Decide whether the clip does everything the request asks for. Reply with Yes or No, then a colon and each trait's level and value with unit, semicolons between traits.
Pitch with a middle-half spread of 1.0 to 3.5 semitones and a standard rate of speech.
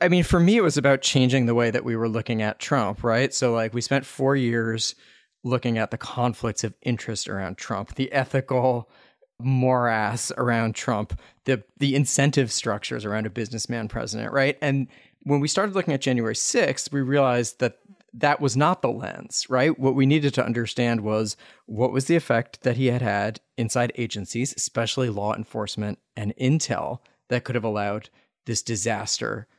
Yes: average, 3.2 semitones; average, 180 wpm